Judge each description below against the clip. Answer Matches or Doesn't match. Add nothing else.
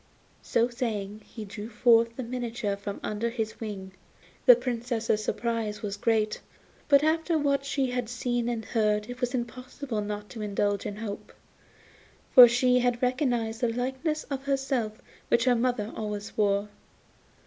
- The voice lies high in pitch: Matches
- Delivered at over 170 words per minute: Doesn't match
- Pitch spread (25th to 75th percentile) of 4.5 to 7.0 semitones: Doesn't match